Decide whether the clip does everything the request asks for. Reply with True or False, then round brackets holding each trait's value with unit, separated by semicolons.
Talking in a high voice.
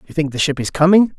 False (160 Hz)